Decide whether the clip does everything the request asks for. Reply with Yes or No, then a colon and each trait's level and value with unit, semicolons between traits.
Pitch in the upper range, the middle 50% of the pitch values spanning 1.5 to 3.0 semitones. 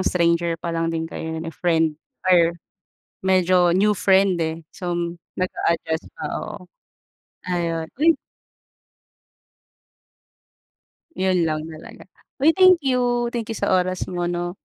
No: medium, 175 Hz; narrow, 2.5 semitones